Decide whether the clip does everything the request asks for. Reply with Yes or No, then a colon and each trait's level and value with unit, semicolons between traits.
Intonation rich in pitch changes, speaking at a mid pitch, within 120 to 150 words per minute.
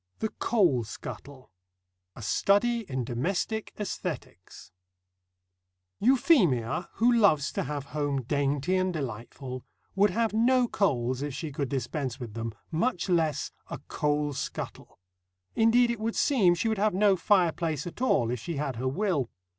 Yes: wide, 8.0 semitones; medium, 160 Hz; average, 145 wpm